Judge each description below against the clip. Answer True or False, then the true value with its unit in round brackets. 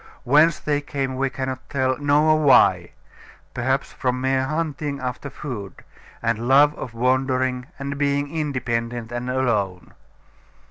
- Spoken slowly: True (130 wpm)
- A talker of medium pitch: False (130 Hz)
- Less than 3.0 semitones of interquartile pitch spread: True (2.4 semitones)